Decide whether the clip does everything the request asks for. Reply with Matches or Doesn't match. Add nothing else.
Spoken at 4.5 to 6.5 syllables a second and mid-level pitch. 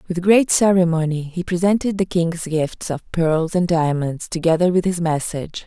Matches